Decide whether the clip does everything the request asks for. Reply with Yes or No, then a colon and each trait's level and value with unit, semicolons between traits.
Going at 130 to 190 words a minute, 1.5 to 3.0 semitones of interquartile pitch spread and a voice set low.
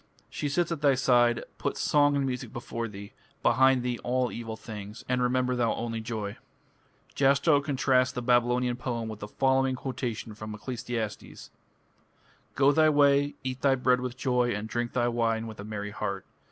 Yes: average, 175 wpm; narrow, 2.6 semitones; low, 125 Hz